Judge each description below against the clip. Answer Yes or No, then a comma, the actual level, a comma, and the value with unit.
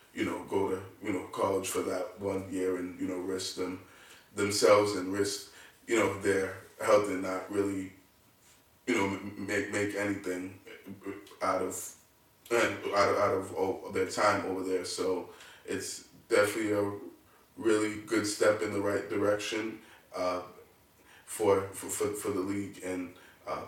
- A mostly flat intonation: Yes, narrow, 1.7 semitones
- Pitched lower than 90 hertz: No, low, 100 Hz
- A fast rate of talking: No, average, 155 wpm